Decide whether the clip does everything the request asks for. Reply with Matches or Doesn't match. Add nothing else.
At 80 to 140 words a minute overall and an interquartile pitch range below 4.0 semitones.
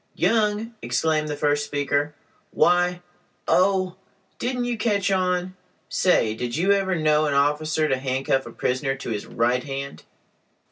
Doesn't match